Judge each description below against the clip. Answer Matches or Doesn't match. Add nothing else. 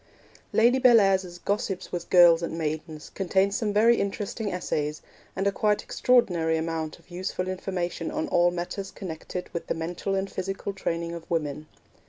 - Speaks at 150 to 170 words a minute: Matches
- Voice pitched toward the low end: Doesn't match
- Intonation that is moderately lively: Matches